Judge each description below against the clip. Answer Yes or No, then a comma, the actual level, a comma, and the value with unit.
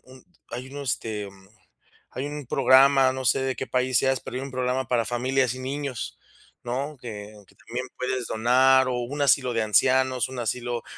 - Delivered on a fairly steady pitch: Yes, narrow, 1.5 semitones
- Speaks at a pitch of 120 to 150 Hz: Yes, low, 130 Hz